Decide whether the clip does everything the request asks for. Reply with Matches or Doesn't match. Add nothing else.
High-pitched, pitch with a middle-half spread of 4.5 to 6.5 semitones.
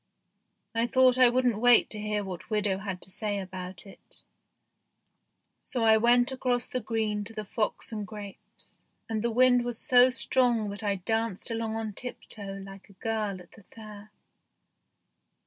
Doesn't match